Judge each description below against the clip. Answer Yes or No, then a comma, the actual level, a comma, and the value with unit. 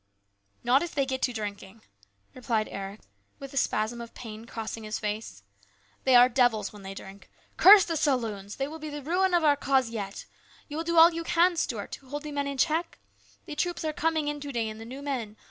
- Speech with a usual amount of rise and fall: No, wide, 5.7 semitones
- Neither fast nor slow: No, fast, 230 wpm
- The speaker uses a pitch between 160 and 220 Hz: No, very high, 255 Hz